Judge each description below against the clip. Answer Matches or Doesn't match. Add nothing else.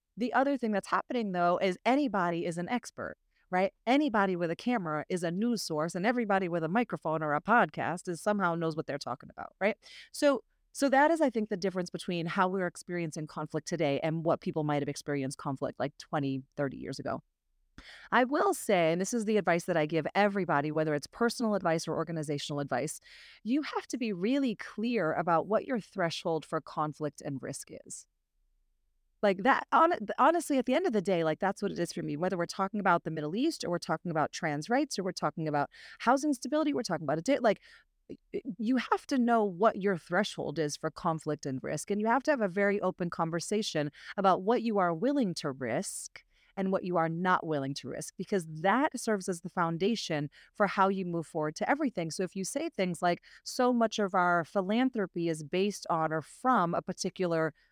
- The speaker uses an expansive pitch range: Matches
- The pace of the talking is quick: Matches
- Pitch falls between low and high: Matches